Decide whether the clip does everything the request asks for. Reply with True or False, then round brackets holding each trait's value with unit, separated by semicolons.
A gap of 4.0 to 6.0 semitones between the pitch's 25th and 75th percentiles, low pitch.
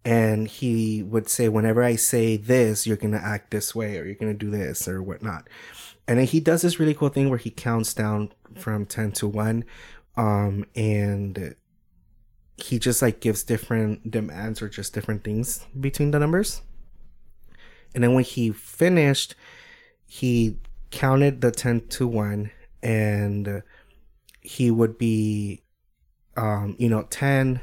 False (2.8 semitones; 110 Hz)